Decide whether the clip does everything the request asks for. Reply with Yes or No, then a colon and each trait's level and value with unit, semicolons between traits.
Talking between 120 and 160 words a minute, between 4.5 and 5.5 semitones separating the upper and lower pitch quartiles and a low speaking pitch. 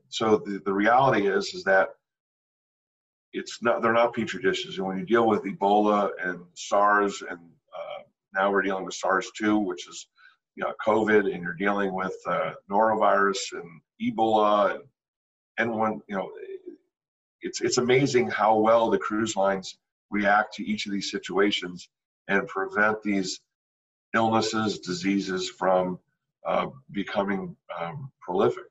No: average, 145 wpm; average, 2.7 semitones; low, 105 Hz